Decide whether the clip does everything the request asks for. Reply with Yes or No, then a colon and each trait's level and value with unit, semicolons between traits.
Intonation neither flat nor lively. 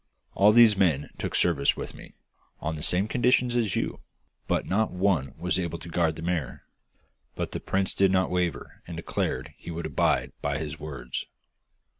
Yes: average, 3.9 semitones